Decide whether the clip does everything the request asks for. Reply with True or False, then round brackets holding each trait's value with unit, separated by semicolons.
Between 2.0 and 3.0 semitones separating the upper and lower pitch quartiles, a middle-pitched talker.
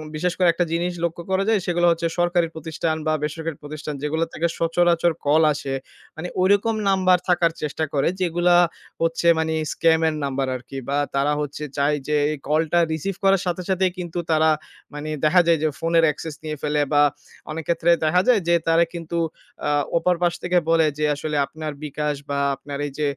True (2.4 semitones; 165 Hz)